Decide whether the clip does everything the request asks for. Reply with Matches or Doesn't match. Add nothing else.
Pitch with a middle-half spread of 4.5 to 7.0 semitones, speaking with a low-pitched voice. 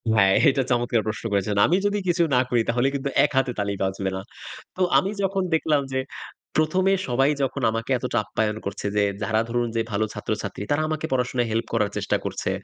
Matches